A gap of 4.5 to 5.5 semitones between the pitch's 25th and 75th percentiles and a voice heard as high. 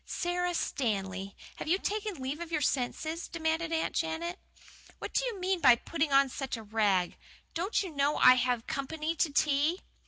Yes: average, 5.1 semitones; very high, 310 Hz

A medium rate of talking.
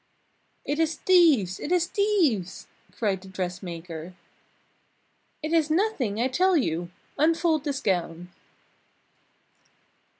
No: slow, 105 wpm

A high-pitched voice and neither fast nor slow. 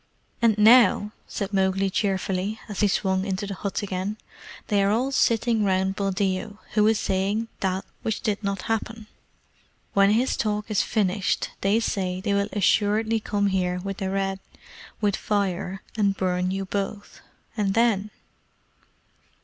Yes: high, 200 Hz; average, 150 wpm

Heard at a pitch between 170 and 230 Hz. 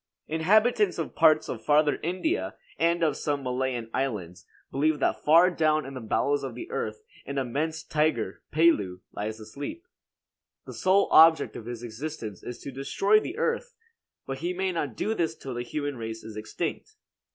No: medium, 150 Hz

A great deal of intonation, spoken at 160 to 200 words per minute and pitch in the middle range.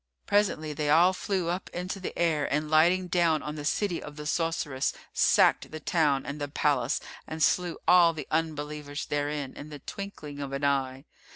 No: average, 2.9 semitones; average, 185 wpm; medium, 155 Hz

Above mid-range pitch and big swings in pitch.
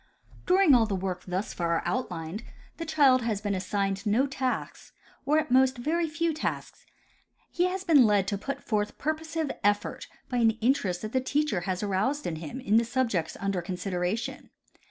Yes: high, 225 Hz; wide, 6.4 semitones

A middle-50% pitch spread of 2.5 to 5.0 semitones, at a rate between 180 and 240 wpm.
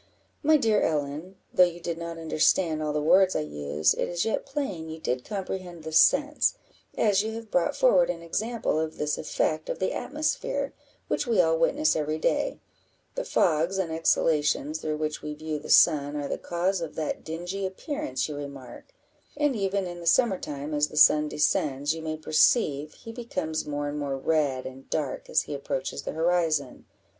Yes: average, 4.3 semitones; average, 190 wpm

